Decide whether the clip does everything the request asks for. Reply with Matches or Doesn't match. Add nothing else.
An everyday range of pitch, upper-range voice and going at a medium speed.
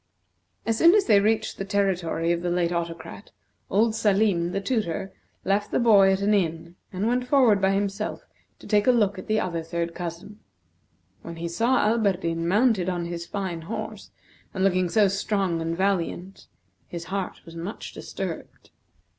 Matches